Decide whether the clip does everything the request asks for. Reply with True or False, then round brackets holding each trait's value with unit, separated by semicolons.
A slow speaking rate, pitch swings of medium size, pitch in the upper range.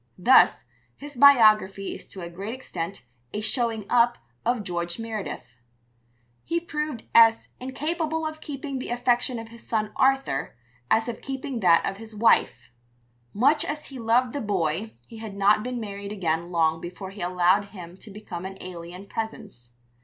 False (165 wpm; 5.0 semitones; 220 Hz)